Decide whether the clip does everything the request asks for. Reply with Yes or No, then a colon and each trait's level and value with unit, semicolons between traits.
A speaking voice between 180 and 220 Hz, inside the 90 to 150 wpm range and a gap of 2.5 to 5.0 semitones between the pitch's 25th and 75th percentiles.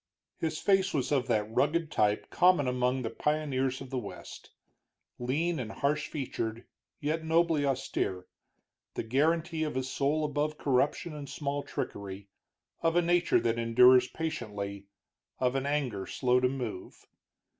No: low, 135 Hz; average, 145 wpm; average, 3.9 semitones